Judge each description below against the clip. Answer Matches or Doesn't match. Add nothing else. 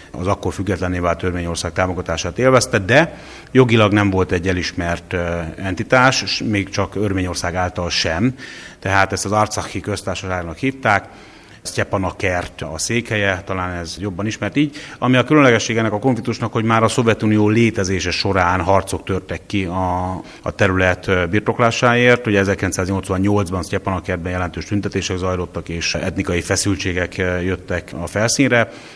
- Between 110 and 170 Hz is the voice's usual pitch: Doesn't match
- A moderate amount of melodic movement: Matches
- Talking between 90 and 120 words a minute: Doesn't match